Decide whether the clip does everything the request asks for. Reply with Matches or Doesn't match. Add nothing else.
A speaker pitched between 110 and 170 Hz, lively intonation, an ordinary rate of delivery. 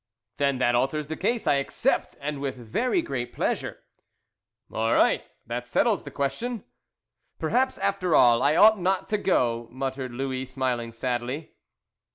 Matches